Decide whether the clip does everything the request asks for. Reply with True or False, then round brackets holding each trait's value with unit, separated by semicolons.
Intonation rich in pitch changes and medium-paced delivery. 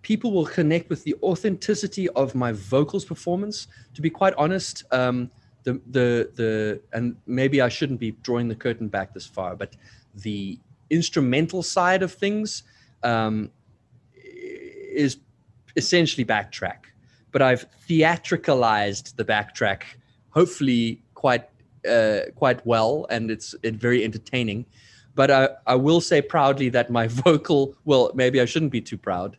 True (5.9 semitones; 145 wpm)